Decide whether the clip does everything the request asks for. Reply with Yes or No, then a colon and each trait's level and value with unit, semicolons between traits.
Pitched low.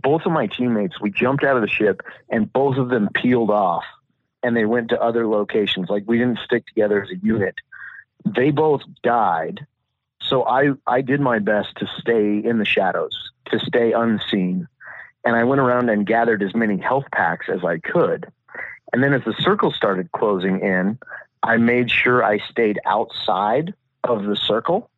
Yes: low, 115 Hz